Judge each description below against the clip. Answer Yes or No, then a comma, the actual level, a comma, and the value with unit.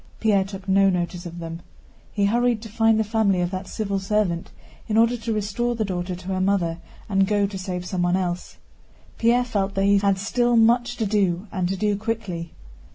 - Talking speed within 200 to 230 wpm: Yes, fast, 205 wpm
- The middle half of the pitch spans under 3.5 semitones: Yes, average, 3.1 semitones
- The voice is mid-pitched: No, high, 200 Hz